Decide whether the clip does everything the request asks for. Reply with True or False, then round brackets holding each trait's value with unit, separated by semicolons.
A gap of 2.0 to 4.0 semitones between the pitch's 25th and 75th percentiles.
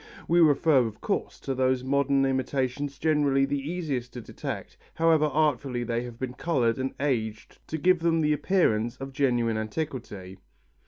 True (3.6 semitones)